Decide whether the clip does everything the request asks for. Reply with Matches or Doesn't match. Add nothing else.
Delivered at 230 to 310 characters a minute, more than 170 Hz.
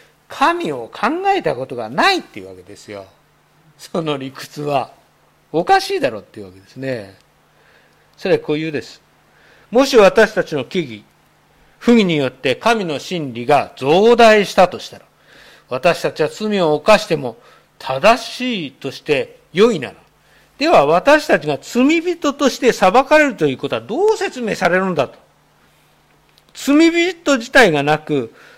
Matches